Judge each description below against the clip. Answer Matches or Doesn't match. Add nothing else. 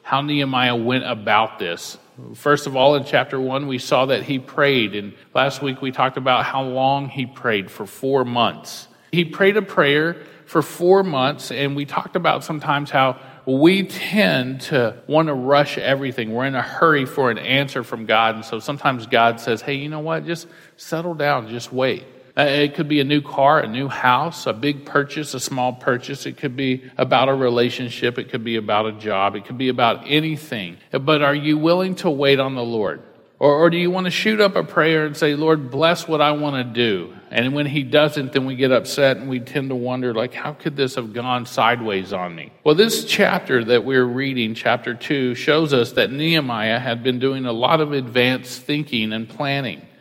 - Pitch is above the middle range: Doesn't match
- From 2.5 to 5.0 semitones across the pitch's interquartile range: Matches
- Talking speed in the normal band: Doesn't match